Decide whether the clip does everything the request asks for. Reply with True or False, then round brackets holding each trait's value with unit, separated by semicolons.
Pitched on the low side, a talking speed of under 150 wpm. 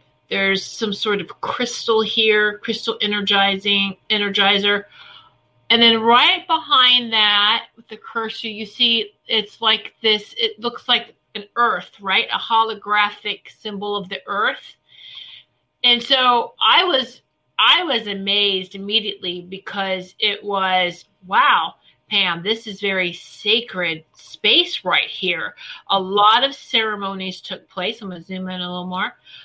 False (210 Hz; 135 wpm)